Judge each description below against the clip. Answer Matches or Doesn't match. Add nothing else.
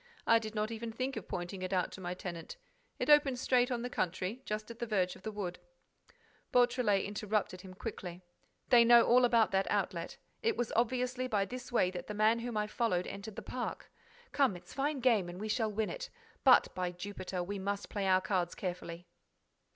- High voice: Matches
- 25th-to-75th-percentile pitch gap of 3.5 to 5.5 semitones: Matches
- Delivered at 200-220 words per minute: Matches